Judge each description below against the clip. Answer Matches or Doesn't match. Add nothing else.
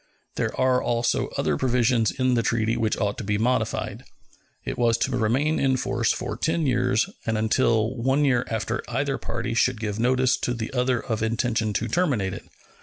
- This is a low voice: Matches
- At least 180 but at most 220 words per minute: Matches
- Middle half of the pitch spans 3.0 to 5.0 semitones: Doesn't match